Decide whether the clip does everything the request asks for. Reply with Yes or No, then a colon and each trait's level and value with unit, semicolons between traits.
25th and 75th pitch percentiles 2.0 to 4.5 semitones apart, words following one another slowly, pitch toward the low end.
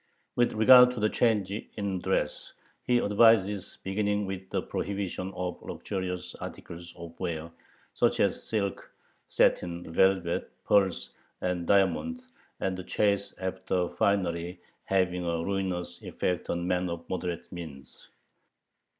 Yes: narrow, 2.5 semitones; slow, 125 wpm; very low, 95 Hz